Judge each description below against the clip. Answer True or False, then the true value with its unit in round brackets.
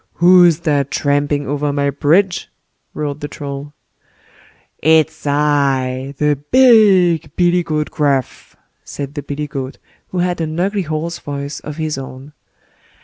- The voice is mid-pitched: True (150 Hz)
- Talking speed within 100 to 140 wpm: True (135 wpm)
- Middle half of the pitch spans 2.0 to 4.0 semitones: True (3.0 semitones)